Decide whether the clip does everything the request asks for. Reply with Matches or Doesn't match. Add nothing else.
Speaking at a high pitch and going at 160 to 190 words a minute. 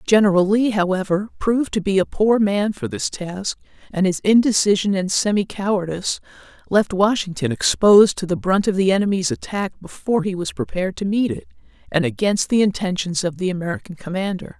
Matches